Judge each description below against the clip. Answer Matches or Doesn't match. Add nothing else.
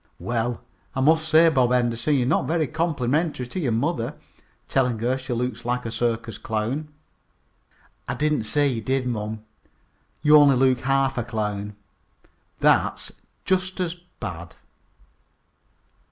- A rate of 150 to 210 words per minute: Doesn't match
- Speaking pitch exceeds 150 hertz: Doesn't match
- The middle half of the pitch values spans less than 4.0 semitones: Doesn't match